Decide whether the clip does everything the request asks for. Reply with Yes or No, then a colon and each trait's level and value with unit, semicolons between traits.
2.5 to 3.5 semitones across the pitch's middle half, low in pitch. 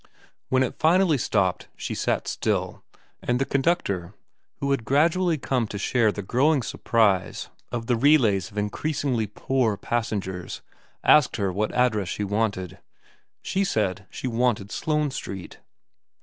No: average, 5.3 semitones; low, 115 Hz